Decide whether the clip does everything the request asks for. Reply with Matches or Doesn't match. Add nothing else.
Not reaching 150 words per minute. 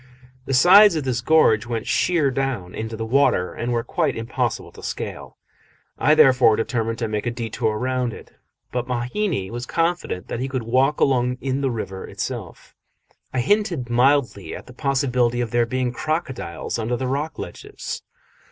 Doesn't match